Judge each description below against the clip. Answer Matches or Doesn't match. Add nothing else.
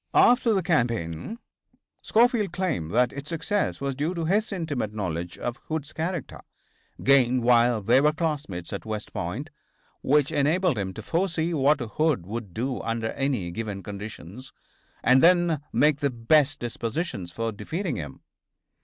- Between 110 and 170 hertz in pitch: Matches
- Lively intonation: Matches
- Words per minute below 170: Matches